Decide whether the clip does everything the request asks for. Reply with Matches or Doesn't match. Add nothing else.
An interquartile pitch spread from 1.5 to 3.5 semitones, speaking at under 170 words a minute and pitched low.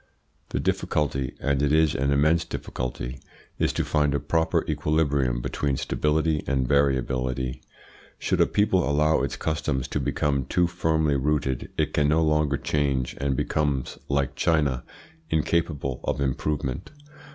Matches